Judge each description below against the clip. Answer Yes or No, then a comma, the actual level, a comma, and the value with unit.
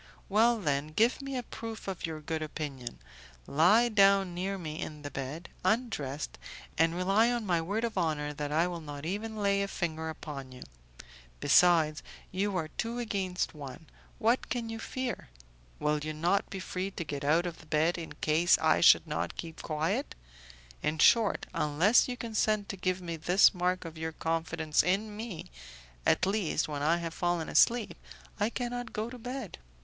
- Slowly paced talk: No, average, 180 wpm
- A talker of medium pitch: Yes, medium, 175 Hz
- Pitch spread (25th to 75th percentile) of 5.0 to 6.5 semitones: Yes, average, 5.3 semitones